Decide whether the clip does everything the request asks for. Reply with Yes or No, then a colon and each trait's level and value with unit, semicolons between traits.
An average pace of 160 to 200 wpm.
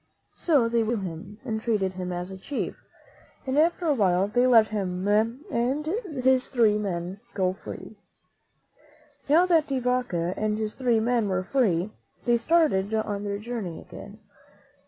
Yes: average, 165 wpm